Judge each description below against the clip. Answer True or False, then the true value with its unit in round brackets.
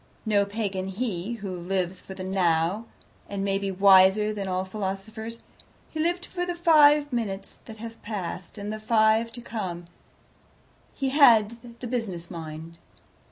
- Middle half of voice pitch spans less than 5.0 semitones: True (3.5 semitones)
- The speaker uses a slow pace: False (155 wpm)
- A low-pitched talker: False (205 Hz)